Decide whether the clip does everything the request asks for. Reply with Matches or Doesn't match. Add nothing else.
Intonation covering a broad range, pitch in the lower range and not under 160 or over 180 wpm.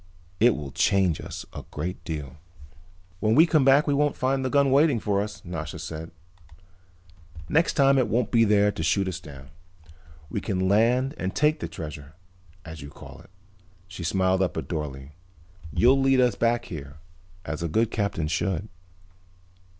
Matches